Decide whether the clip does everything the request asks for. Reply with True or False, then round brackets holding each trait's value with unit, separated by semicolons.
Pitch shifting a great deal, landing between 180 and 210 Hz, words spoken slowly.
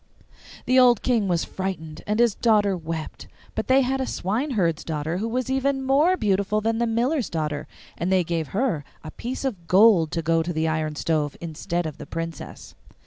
False (6.7 semitones; 190 Hz; 195 wpm)